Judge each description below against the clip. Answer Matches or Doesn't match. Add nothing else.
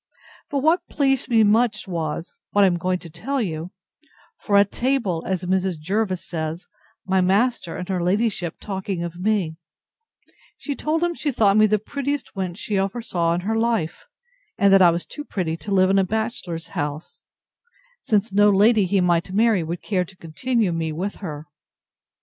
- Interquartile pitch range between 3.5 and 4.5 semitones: Matches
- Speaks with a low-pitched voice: Doesn't match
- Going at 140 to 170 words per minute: Doesn't match